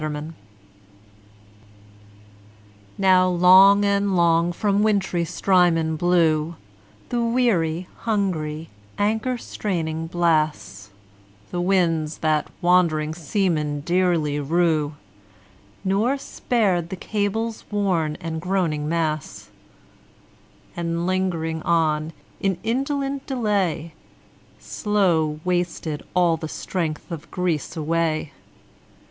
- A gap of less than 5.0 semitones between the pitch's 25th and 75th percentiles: Yes, average, 3.7 semitones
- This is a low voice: No, medium, 175 Hz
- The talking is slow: Yes, slow, 95 wpm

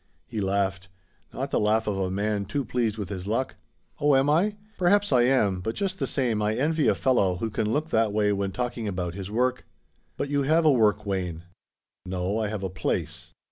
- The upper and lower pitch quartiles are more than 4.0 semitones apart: Yes, average, 5.3 semitones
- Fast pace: Yes, fast, 215 wpm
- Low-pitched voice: Yes, low, 110 Hz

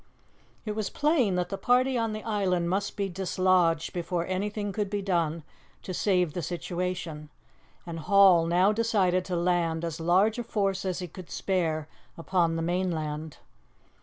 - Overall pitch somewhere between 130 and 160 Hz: No, medium, 185 Hz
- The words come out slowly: No, average, 165 wpm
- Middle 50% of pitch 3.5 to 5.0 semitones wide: No, average, 3.0 semitones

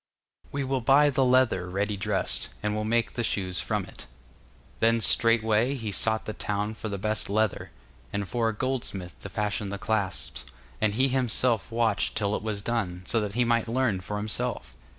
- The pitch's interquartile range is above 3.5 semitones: No, narrow, 2.6 semitones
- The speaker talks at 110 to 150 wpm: No, average, 190 wpm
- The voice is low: Yes, low, 110 Hz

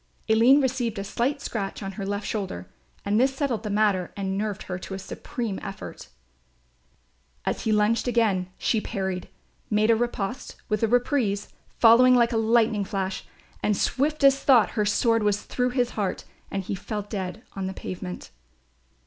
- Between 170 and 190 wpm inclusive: Yes, average, 175 wpm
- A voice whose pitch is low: No, high, 215 Hz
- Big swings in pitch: No, average, 3.4 semitones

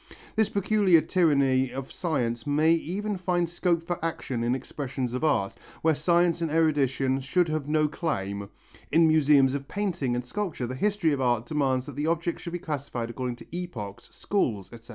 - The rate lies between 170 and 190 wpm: Yes, average, 180 wpm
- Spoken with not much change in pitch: No, average, 4.9 semitones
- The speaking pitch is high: No, medium, 150 Hz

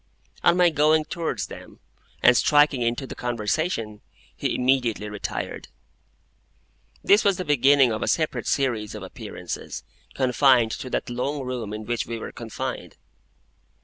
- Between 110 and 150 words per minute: Yes, average, 145 wpm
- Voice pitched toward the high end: No, low, 130 Hz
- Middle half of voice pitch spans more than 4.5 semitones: No, average, 4.2 semitones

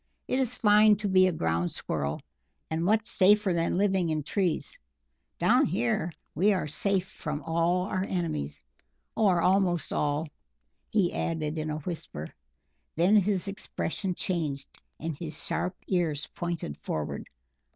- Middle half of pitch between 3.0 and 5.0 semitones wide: Yes, average, 4.0 semitones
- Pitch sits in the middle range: Yes, medium, 175 Hz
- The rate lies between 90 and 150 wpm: Yes, average, 140 wpm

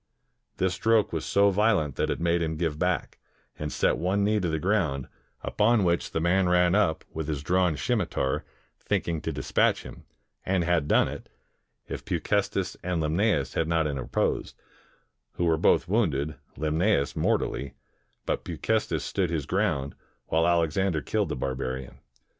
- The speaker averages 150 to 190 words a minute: Yes, average, 165 wpm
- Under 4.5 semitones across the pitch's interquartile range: Yes, average, 3.7 semitones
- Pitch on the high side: No, very low, 85 Hz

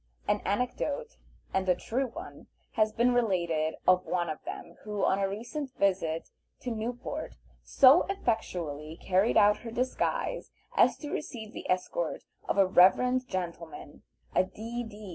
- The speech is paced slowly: No, average, 145 wpm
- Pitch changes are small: No, average, 5.1 semitones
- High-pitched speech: Yes, high, 210 Hz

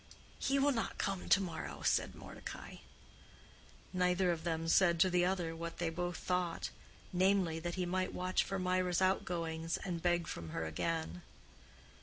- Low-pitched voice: No, medium, 175 Hz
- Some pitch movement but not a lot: No, narrow, 2.0 semitones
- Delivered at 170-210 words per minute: No, average, 160 wpm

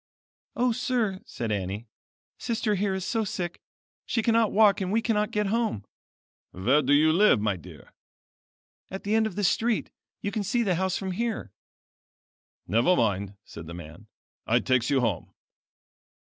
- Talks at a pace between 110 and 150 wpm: No, average, 165 wpm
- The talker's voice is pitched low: No, high, 190 Hz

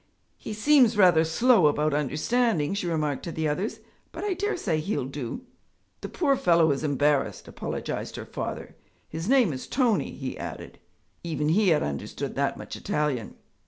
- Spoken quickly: No, average, 165 wpm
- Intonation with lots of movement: Yes, wide, 7.1 semitones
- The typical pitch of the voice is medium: Yes, medium, 165 Hz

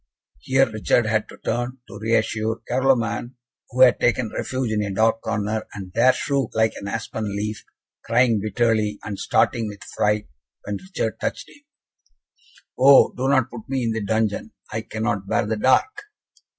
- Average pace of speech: Yes, average, 165 wpm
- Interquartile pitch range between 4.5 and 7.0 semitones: No, average, 2.8 semitones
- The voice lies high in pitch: No, low, 115 Hz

